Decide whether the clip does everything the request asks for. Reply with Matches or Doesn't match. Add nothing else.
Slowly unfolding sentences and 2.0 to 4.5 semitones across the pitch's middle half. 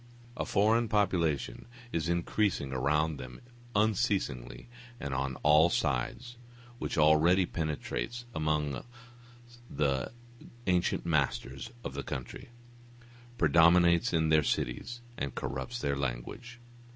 Doesn't match